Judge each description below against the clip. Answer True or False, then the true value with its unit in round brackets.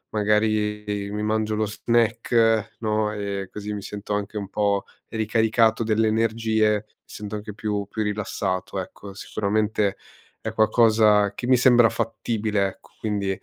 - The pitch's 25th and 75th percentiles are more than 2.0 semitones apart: False (1.2 semitones)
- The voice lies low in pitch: True (105 Hz)